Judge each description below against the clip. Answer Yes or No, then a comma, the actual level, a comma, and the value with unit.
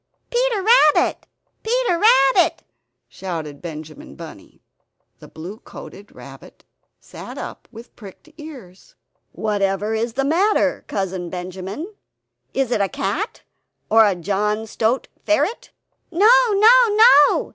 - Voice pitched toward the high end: Yes, high, 225 Hz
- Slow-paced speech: Yes, slow, 115 wpm